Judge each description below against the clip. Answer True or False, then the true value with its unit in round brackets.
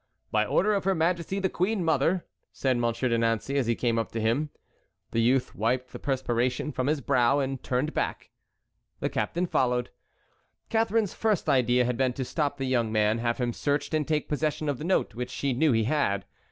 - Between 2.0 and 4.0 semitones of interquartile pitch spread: False (4.4 semitones)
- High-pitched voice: False (130 Hz)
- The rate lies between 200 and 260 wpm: True (205 wpm)